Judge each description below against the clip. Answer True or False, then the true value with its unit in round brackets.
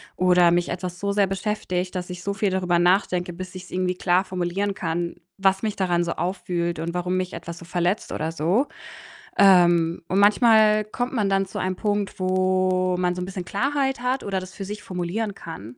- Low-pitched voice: False (185 Hz)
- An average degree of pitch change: False (2.2 semitones)